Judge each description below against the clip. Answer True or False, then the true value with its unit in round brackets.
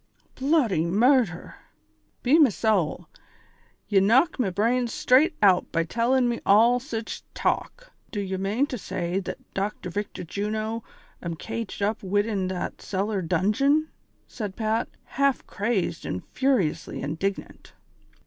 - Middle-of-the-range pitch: False (215 Hz)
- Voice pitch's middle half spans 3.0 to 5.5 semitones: True (4.5 semitones)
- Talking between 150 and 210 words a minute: False (140 wpm)